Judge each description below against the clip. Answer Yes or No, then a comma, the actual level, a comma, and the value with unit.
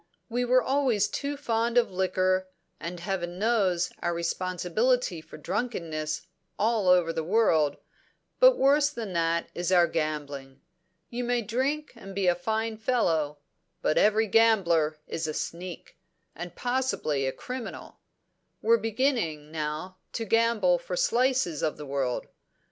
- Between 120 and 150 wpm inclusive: Yes, average, 140 wpm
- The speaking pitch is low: No, medium, 185 Hz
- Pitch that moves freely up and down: Yes, wide, 6.0 semitones